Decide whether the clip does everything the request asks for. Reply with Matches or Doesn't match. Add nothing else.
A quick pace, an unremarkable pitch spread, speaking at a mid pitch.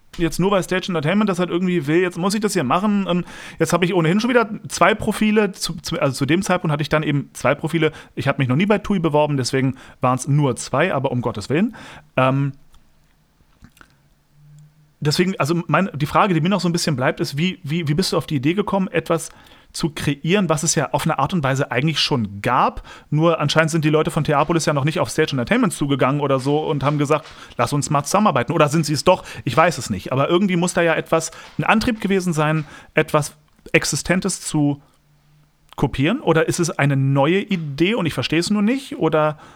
Matches